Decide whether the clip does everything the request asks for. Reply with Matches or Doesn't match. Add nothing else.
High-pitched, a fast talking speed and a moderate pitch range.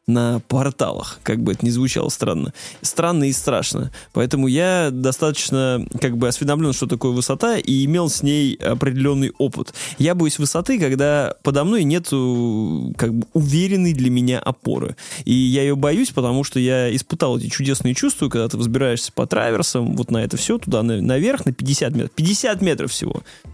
Doesn't match